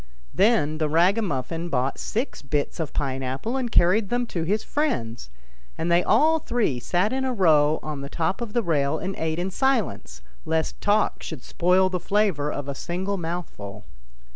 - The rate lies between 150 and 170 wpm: No, average, 180 wpm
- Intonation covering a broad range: Yes, wide, 6.2 semitones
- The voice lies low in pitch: No, medium, 175 Hz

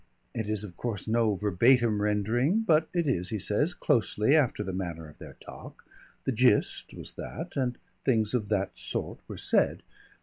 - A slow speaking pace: No, average, 175 wpm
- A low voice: Yes, low, 110 Hz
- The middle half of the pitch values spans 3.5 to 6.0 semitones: Yes, average, 4.2 semitones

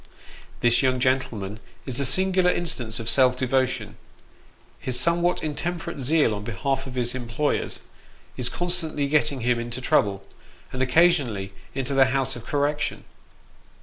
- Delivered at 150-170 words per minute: No, average, 140 wpm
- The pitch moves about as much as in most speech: Yes, average, 3.6 semitones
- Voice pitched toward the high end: No, low, 130 Hz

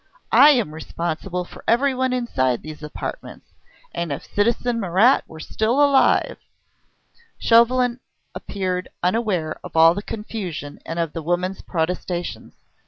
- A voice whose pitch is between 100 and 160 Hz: No, medium, 185 Hz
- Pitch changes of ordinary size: No, wide, 6.3 semitones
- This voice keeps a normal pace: No, slow, 130 wpm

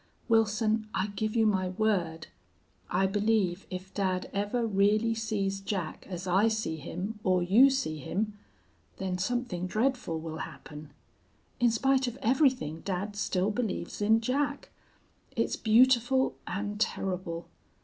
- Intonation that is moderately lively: Yes, average, 3.6 semitones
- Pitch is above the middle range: Yes, high, 205 Hz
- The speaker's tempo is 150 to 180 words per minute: No, slow, 135 wpm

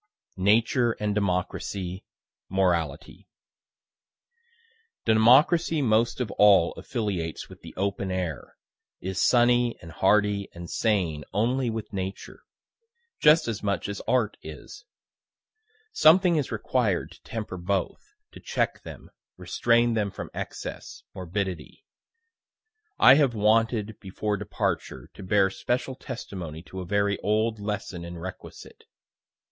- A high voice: No, low, 105 Hz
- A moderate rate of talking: No, slow, 120 wpm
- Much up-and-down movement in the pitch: No, average, 3.9 semitones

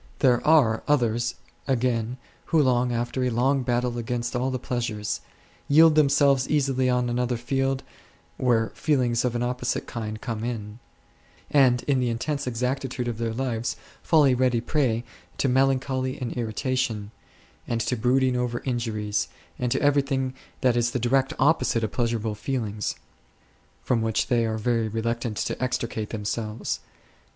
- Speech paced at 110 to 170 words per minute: Yes, average, 150 wpm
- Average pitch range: No, narrow, 2.3 semitones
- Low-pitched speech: Yes, low, 125 Hz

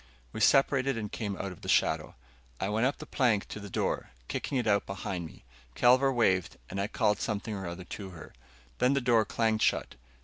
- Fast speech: Yes, fast, 210 wpm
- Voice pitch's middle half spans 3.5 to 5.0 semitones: Yes, average, 4.1 semitones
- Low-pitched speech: Yes, low, 110 Hz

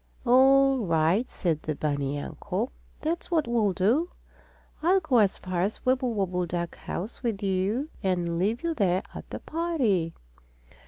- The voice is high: Yes, high, 205 Hz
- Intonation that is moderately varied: No, wide, 6.8 semitones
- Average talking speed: Yes, average, 155 wpm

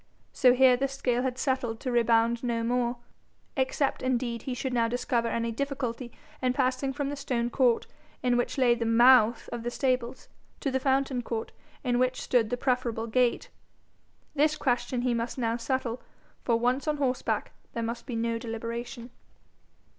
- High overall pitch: Yes, high, 245 Hz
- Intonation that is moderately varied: No, narrow, 1.9 semitones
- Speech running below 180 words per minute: Yes, average, 170 wpm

